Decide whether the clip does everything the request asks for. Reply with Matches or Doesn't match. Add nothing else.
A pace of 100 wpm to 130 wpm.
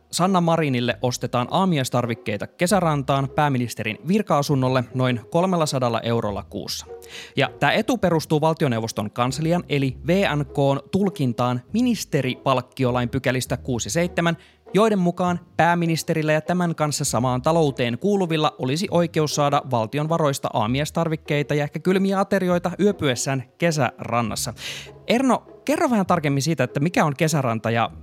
Matches